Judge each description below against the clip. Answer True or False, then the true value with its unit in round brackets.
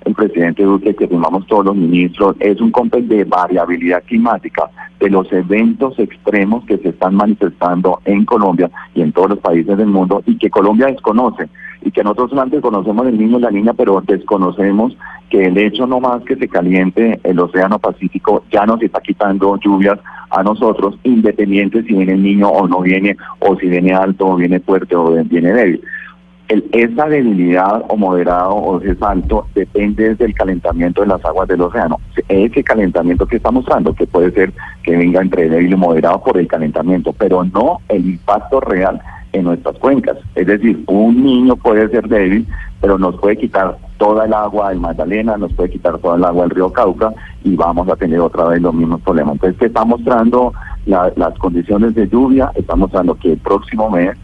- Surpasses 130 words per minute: True (190 wpm)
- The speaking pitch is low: True (100 Hz)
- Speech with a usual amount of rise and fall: True (3.5 semitones)